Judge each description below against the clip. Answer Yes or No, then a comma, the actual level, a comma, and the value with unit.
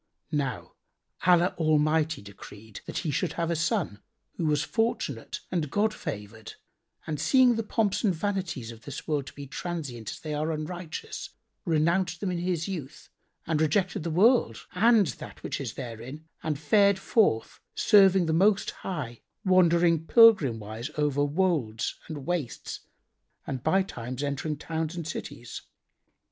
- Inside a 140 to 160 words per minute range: Yes, average, 150 wpm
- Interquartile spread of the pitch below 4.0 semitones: No, average, 4.8 semitones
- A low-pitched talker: No, medium, 160 Hz